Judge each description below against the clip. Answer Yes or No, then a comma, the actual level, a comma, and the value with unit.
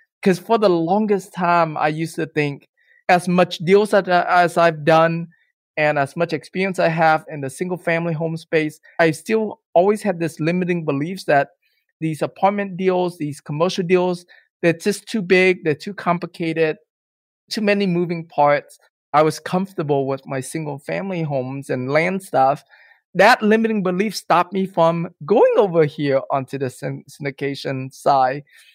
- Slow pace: No, average, 160 wpm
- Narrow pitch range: No, average, 3.8 semitones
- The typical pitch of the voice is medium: Yes, medium, 170 Hz